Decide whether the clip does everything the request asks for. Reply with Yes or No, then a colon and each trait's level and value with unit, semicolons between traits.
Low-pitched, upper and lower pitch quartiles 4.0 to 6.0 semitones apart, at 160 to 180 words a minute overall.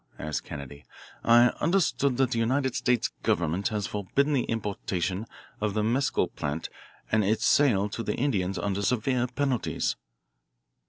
No: low, 110 Hz; average, 4.6 semitones; average, 145 wpm